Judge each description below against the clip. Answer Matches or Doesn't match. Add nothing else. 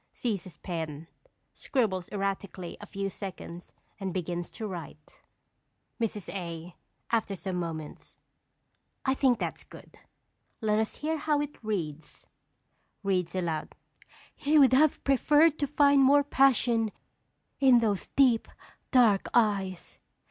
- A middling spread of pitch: Doesn't match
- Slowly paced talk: Matches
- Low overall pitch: Doesn't match